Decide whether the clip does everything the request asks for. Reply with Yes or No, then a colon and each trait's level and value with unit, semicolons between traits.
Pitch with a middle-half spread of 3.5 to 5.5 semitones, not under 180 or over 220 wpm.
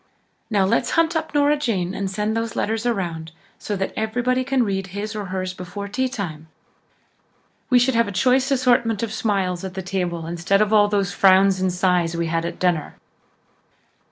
Yes: average, 4.0 semitones; average, 185 wpm